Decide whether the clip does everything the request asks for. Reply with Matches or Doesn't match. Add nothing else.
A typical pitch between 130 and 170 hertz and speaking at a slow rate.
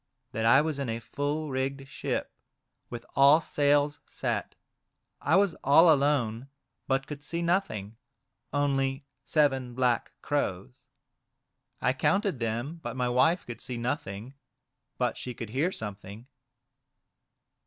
Matches